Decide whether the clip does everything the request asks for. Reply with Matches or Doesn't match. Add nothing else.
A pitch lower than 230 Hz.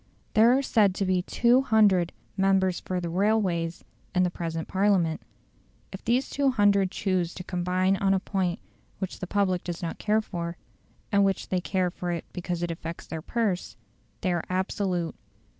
Matches